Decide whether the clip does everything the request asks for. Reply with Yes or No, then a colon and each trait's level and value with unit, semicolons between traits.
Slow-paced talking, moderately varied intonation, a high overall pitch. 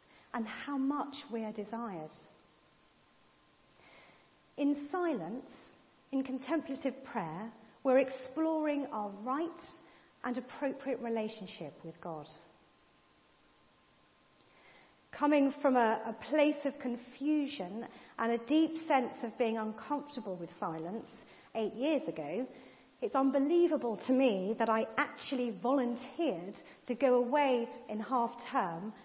Yes: slow, 110 wpm; average, 4.3 semitones; very high, 250 Hz